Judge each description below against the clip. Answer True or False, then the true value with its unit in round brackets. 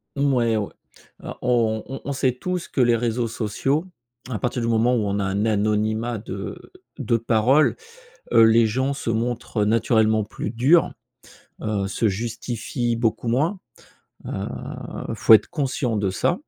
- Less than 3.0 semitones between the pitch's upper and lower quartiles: True (2.5 semitones)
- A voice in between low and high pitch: False (115 Hz)